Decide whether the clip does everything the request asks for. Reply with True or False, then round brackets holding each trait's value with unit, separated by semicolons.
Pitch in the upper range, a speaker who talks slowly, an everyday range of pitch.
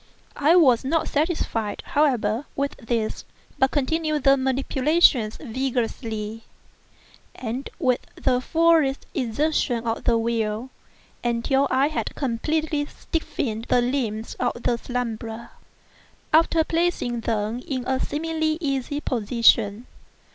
True (255 Hz; 110 wpm; 4.4 semitones)